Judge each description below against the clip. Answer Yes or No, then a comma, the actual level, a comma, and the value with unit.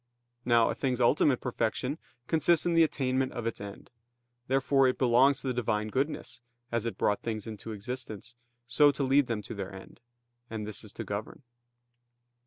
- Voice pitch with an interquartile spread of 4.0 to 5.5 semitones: No, average, 3.6 semitones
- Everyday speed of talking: Yes, average, 180 wpm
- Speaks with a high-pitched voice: No, low, 120 Hz